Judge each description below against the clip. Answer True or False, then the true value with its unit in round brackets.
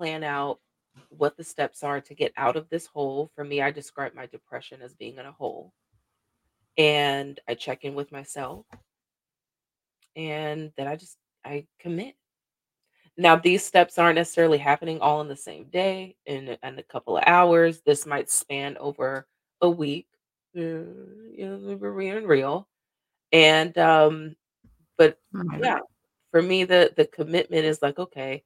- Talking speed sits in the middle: True (160 wpm)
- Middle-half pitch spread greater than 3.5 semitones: False (3.1 semitones)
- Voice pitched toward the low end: False (155 Hz)